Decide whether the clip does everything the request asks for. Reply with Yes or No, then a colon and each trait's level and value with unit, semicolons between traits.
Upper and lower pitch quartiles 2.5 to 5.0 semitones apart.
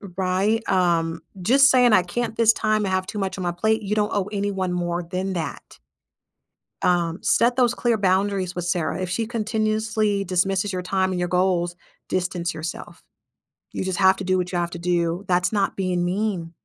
Yes: average, 3.0 semitones